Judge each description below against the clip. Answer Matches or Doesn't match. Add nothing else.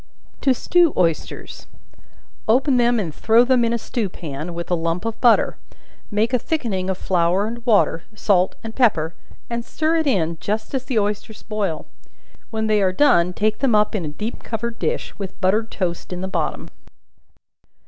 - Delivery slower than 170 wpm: Doesn't match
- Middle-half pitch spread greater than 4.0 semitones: Matches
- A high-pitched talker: Matches